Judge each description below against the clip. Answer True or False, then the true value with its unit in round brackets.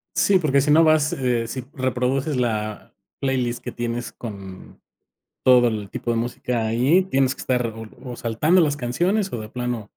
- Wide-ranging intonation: False (3.3 semitones)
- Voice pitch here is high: False (125 Hz)